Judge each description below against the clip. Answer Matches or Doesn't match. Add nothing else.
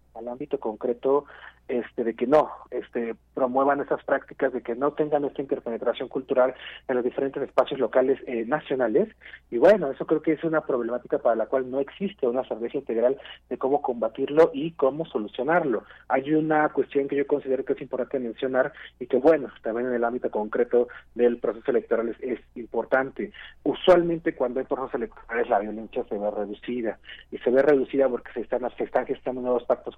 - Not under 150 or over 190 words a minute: Matches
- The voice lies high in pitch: Doesn't match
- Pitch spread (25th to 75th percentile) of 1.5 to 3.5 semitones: Matches